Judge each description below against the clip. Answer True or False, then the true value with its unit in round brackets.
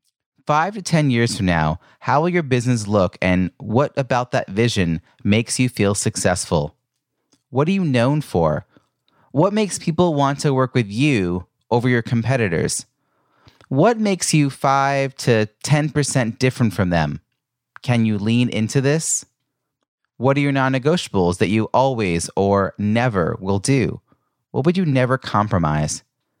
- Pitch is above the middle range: False (125 Hz)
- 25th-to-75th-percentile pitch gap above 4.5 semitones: True (5.1 semitones)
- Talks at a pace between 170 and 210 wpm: False (150 wpm)